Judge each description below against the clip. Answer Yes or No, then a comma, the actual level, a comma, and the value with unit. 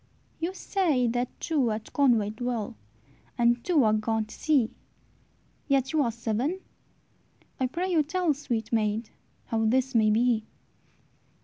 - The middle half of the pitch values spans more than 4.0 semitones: Yes, average, 4.8 semitones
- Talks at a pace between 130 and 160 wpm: Yes, average, 140 wpm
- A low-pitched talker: No, high, 245 Hz